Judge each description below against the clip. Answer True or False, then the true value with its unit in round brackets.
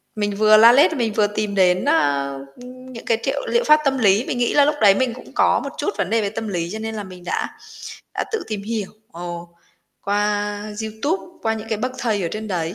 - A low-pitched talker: False (215 Hz)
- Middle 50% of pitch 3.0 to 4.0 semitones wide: True (3.3 semitones)